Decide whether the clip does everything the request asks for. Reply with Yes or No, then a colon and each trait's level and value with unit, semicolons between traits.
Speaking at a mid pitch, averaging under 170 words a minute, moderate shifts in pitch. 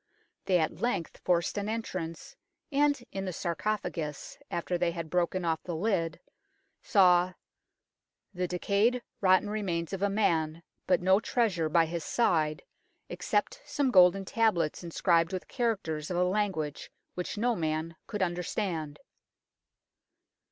Yes: medium, 180 Hz; slow, 135 wpm; average, 3.7 semitones